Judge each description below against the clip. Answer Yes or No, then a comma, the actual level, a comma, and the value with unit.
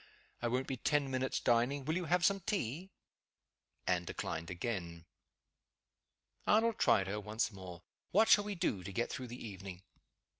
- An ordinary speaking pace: Yes, average, 160 wpm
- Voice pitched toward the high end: No, low, 120 Hz